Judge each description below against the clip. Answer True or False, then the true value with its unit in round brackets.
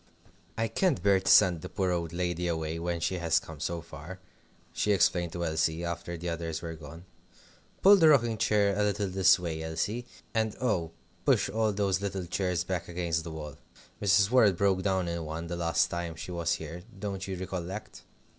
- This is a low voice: True (90 Hz)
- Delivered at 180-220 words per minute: True (195 wpm)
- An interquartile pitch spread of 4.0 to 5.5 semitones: False (3.1 semitones)